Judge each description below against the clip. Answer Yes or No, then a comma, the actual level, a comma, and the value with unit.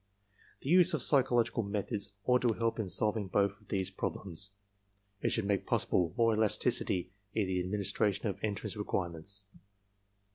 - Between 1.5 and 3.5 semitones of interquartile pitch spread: Yes, average, 2.8 semitones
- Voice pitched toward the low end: Yes, low, 100 Hz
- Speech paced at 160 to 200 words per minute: No, average, 150 wpm